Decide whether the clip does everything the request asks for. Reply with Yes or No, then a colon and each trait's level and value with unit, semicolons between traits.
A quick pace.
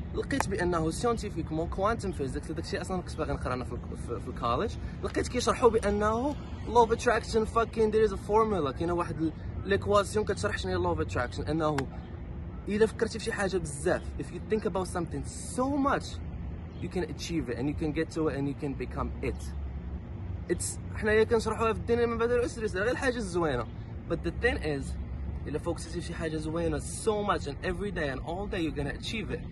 Yes: fast, 200 wpm